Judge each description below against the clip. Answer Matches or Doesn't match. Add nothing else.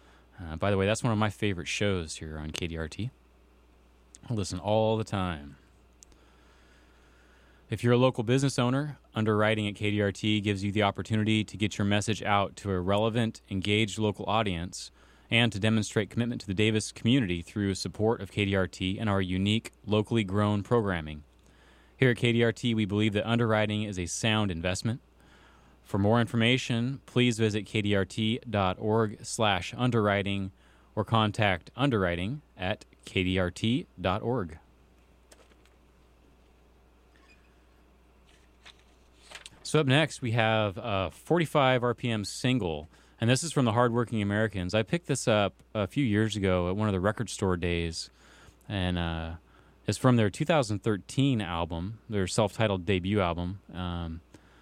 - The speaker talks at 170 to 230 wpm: Doesn't match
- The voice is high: Doesn't match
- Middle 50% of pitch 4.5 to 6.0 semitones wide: Matches